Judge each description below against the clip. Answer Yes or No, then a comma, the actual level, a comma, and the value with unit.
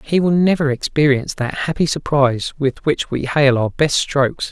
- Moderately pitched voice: Yes, medium, 145 Hz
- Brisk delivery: No, average, 185 wpm